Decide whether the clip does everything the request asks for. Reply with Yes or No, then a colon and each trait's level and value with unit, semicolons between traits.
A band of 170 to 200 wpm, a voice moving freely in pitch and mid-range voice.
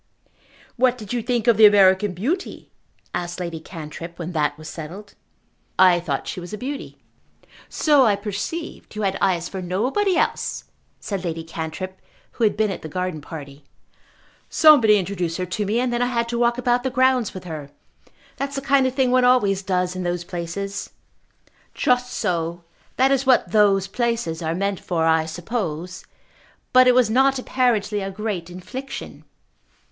No: average, 175 wpm; wide, 5.9 semitones; high, 200 Hz